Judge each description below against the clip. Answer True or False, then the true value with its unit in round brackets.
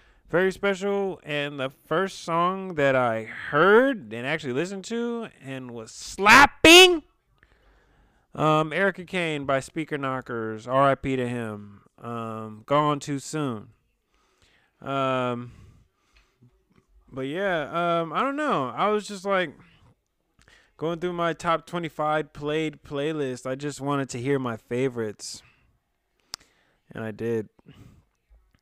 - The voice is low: False (145 Hz)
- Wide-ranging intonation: True (5.9 semitones)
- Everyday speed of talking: False (120 wpm)